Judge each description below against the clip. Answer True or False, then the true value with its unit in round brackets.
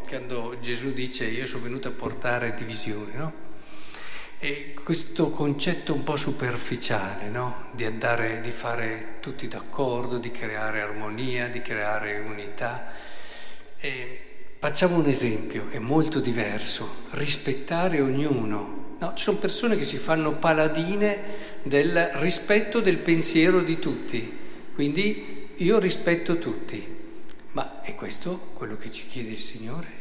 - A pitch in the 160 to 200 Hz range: False (135 Hz)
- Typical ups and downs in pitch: False (5.8 semitones)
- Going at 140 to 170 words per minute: False (130 wpm)